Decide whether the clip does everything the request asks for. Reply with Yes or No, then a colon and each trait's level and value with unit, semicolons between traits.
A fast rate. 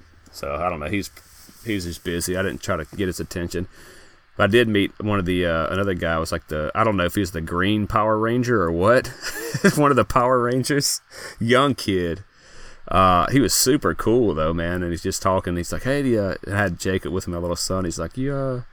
Yes: fast, 240 wpm